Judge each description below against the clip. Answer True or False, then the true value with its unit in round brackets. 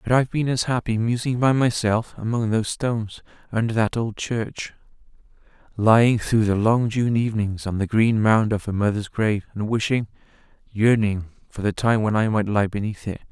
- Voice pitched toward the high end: False (110 Hz)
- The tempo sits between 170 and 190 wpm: True (180 wpm)